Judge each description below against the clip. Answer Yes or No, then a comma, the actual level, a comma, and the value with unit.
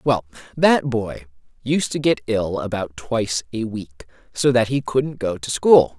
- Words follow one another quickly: No, average, 180 wpm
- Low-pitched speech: Yes, low, 120 Hz